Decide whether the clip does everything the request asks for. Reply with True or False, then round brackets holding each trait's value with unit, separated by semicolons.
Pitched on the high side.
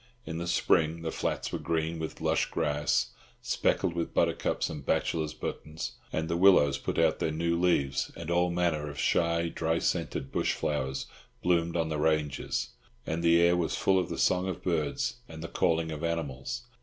False (80 Hz)